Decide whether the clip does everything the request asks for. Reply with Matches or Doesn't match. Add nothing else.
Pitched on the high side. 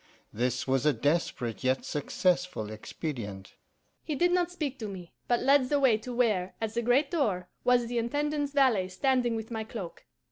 Matches